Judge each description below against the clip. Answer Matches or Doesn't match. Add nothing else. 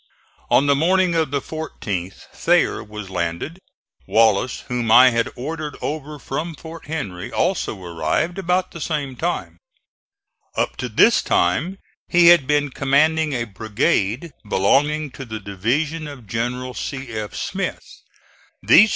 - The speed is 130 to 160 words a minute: Matches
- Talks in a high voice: Doesn't match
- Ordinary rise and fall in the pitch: Doesn't match